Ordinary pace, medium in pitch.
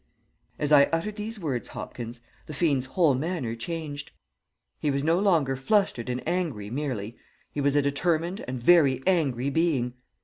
Yes: average, 160 wpm; medium, 145 Hz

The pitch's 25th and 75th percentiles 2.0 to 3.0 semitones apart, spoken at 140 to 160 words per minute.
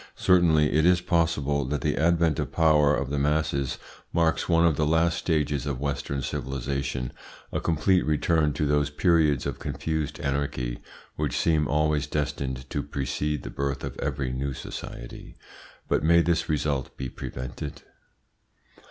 Yes: narrow, 2.6 semitones; average, 150 wpm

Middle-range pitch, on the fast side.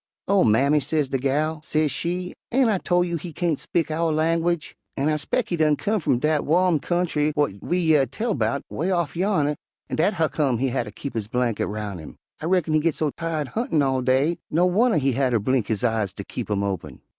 Yes: medium, 155 Hz; fast, 225 wpm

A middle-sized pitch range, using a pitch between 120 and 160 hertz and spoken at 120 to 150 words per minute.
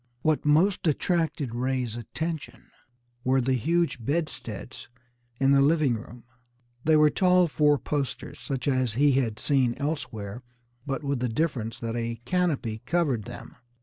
Yes: average, 4.5 semitones; low, 135 Hz; average, 145 wpm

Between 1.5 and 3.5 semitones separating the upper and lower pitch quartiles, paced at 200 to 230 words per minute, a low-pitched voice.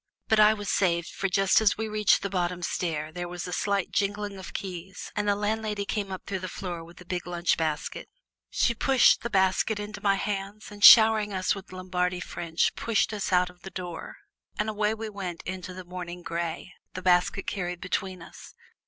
No: narrow, 2.6 semitones; fast, 205 wpm; high, 190 Hz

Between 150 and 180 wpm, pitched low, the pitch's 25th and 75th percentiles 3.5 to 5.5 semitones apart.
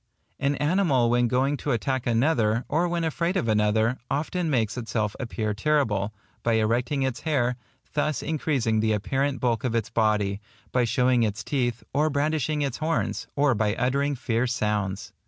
Yes: average, 165 wpm; low, 125 Hz; average, 4.4 semitones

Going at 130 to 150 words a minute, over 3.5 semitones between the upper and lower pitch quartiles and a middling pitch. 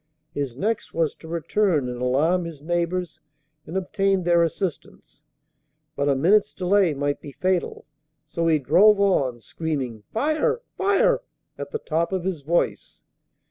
Yes: average, 145 wpm; average, 5.0 semitones; medium, 170 Hz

